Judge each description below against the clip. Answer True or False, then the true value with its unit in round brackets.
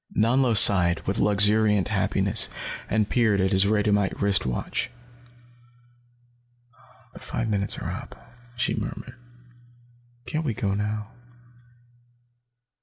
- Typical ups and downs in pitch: False (1.9 semitones)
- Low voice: True (105 Hz)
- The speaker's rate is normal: False (110 wpm)